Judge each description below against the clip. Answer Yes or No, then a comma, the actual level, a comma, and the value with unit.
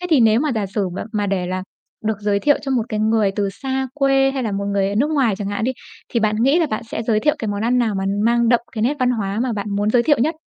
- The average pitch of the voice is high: Yes, high, 225 Hz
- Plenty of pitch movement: No, average, 4.2 semitones